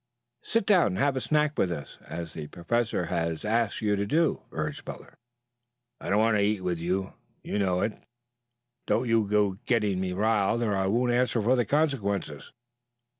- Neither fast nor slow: Yes, average, 190 wpm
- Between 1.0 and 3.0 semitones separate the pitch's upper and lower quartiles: No, average, 4.3 semitones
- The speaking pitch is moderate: No, low, 105 Hz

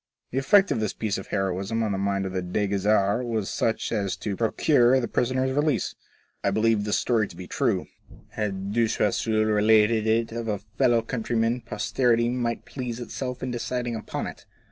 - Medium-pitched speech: No, low, 110 Hz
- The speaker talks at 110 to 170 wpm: No, average, 190 wpm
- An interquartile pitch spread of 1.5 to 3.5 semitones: Yes, average, 2.8 semitones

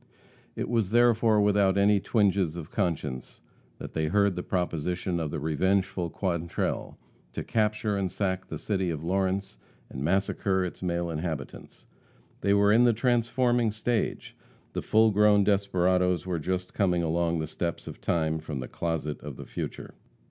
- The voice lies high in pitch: No, very low, 95 Hz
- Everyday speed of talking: Yes, average, 160 wpm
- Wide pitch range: No, average, 3.5 semitones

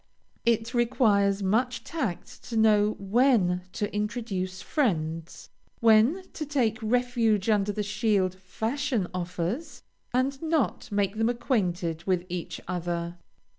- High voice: Yes, high, 210 Hz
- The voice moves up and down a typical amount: Yes, average, 4.6 semitones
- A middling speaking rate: No, slow, 120 wpm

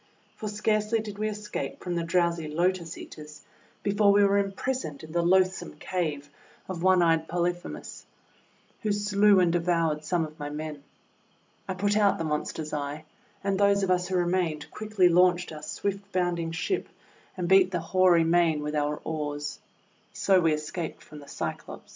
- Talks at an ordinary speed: Yes, average, 175 wpm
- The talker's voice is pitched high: No, medium, 175 Hz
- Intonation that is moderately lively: Yes, average, 3.9 semitones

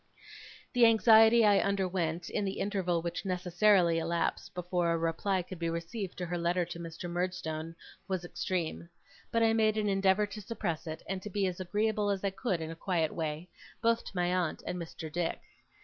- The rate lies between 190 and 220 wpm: Yes, average, 195 wpm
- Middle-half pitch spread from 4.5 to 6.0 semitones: No, average, 3.2 semitones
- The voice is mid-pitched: Yes, medium, 180 Hz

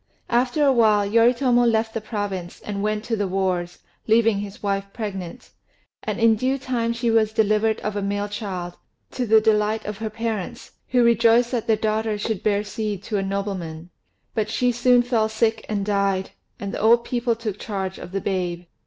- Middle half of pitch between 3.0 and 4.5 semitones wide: No, narrow, 2.6 semitones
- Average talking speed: Yes, average, 190 wpm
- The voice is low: No, high, 215 Hz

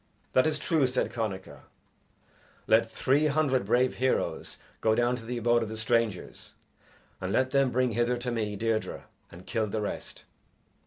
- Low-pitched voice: Yes, low, 120 Hz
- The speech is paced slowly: No, average, 165 wpm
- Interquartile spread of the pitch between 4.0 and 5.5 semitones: No, average, 2.7 semitones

